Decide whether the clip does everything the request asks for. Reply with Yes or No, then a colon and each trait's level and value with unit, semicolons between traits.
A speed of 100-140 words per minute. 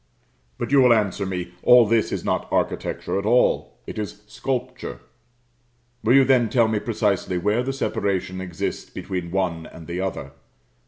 No: average, 165 wpm